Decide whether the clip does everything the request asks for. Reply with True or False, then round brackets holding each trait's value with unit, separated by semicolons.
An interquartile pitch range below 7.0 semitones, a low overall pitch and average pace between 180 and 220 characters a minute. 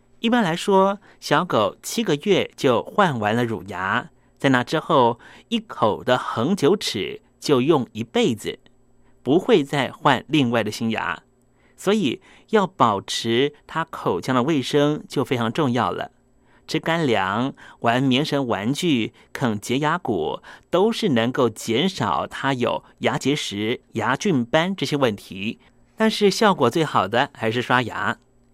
True (5.4 semitones; 130 Hz; 205 characters per minute)